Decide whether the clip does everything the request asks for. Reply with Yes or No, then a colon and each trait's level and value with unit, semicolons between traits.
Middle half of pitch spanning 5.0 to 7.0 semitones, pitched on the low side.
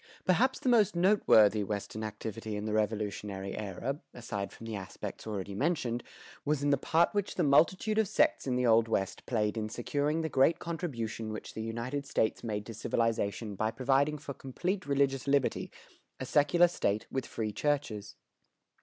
Yes: wide, 5.5 semitones; low, 120 Hz